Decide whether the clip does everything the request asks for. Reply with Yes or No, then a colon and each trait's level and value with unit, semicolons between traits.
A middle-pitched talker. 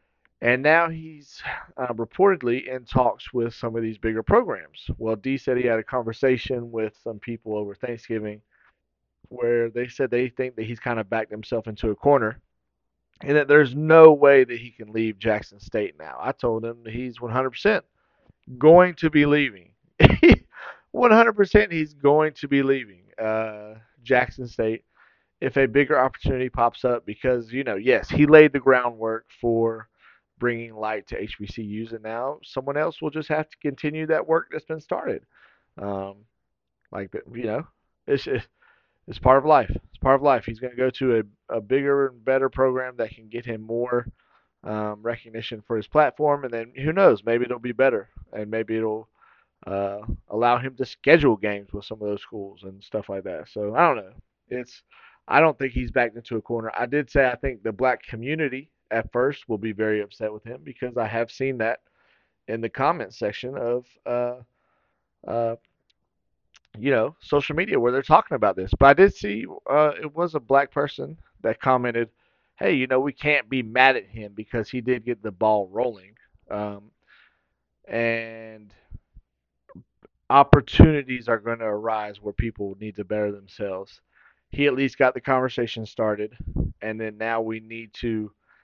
No: low, 120 Hz